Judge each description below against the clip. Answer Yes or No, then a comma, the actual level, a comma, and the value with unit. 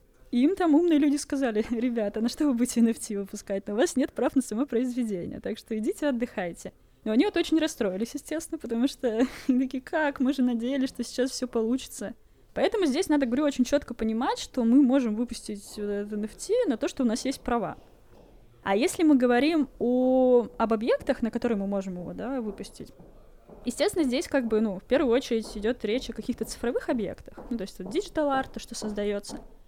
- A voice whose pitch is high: Yes, high, 245 Hz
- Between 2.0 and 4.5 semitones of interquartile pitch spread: Yes, average, 3.7 semitones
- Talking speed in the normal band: No, fast, 200 wpm